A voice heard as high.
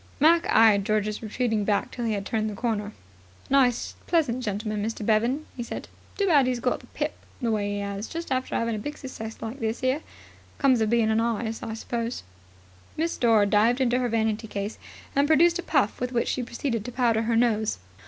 Yes: high, 230 Hz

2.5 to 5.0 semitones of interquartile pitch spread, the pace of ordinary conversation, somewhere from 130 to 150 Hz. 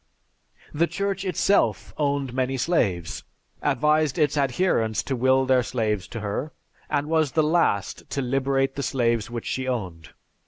Yes: average, 4.3 semitones; average, 150 wpm; low, 135 Hz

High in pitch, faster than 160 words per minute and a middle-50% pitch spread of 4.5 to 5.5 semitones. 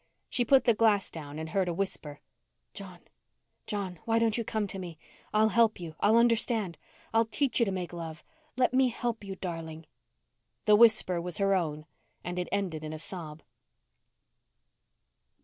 Yes: high, 195 Hz; average, 170 wpm; average, 5.1 semitones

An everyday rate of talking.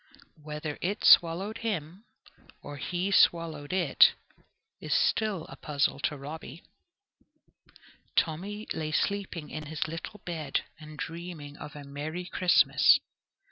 No: slow, 120 wpm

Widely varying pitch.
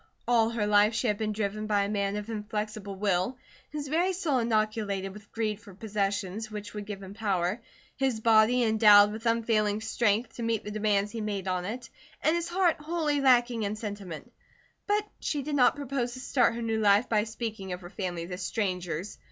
No: average, 2.7 semitones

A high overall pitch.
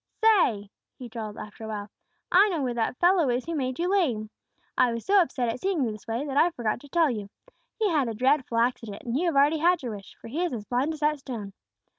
Yes: very high, 255 Hz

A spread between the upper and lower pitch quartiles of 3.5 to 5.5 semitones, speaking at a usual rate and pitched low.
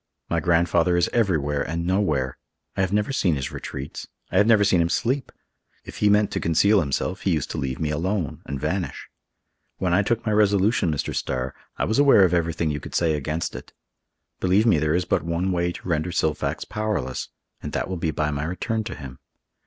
No: average, 4.8 semitones; fast, 210 wpm; very low, 85 Hz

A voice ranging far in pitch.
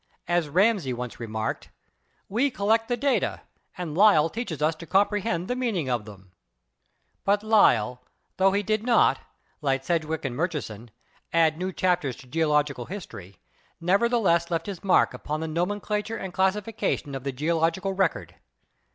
Yes: wide, 5.7 semitones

